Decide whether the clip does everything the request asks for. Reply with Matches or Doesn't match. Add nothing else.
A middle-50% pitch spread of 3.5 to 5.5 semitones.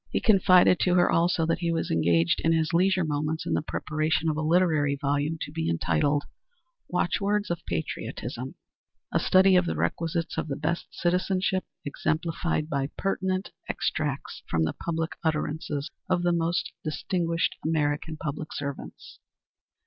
Doesn't match